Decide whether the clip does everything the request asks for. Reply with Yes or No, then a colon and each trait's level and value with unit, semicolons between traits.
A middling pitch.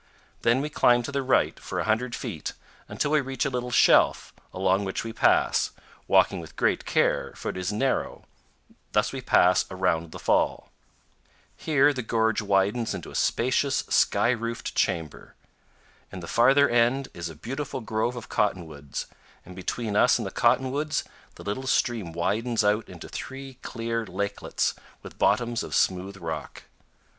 No: low, 115 Hz